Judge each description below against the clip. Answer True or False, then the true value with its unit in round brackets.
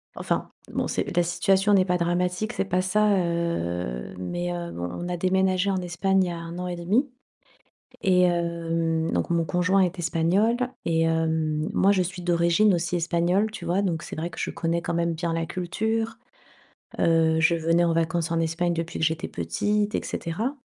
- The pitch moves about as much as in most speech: False (2.0 semitones)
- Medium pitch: True (175 Hz)